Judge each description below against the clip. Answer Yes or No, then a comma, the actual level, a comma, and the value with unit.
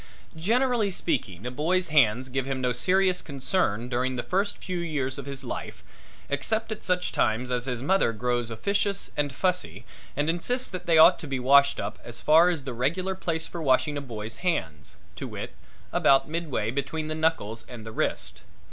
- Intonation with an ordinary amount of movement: No, wide, 6.3 semitones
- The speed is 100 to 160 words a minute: No, average, 190 wpm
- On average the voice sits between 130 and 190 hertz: Yes, medium, 140 Hz